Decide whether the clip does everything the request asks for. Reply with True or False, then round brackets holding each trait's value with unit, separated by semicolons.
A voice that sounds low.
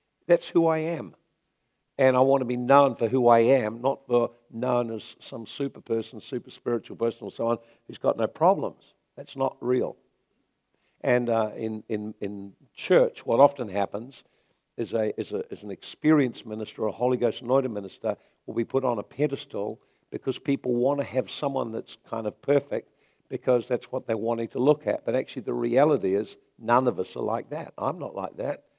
True (120 Hz)